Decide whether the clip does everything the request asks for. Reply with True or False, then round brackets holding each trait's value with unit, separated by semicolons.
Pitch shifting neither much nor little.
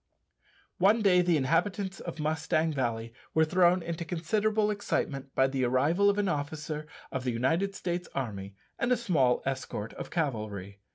False (5.9 semitones)